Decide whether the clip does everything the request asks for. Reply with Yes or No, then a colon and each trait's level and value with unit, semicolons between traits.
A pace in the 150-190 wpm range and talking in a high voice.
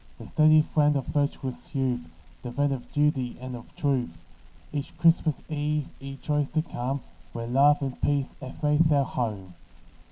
No: average, 165 wpm; medium, 140 Hz